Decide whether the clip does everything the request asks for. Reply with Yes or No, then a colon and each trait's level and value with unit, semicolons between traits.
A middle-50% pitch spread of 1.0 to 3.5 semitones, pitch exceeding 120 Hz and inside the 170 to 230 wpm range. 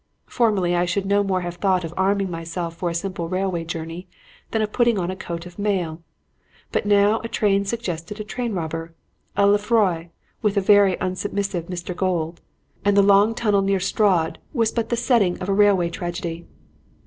Yes: average, 3.0 semitones; high, 190 Hz; average, 185 wpm